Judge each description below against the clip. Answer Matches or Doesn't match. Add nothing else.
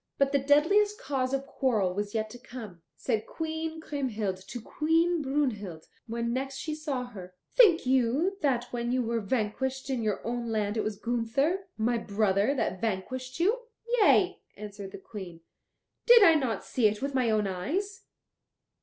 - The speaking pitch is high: Matches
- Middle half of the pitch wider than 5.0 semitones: Matches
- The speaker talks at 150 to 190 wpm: Matches